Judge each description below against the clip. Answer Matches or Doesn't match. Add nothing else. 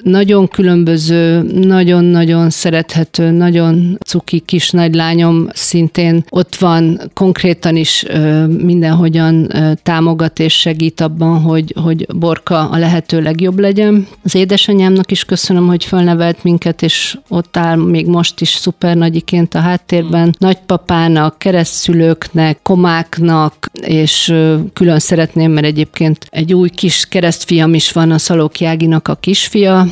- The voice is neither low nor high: Matches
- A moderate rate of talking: Matches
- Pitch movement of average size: Doesn't match